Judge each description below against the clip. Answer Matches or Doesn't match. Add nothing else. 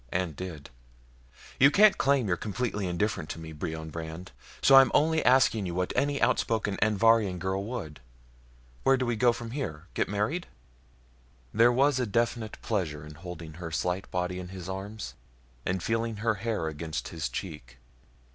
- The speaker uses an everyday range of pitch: Doesn't match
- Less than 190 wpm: Matches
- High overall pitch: Doesn't match